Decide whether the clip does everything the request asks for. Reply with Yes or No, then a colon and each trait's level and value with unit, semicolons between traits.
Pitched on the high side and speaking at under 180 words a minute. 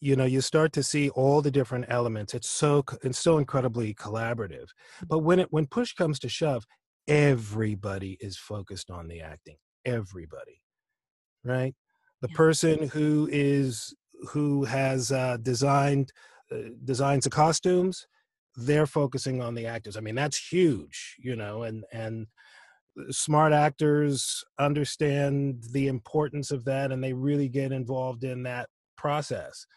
No: low, 135 Hz; average, 145 wpm